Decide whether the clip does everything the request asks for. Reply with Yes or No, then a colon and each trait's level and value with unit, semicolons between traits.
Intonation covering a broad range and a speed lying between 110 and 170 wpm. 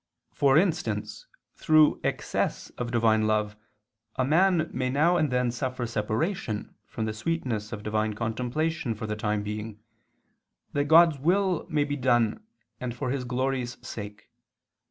Yes: wide, 6.0 semitones; average, 145 wpm